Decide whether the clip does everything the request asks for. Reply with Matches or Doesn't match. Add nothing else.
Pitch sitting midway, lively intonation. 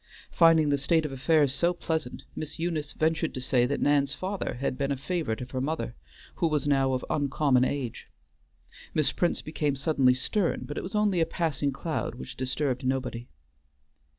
Doesn't match